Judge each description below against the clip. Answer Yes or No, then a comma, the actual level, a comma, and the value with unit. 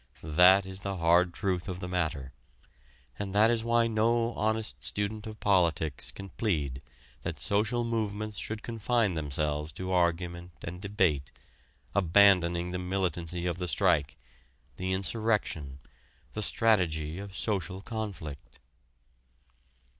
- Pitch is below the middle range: Yes, very low, 95 Hz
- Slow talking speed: Yes, slow, 125 wpm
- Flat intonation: No, average, 3.9 semitones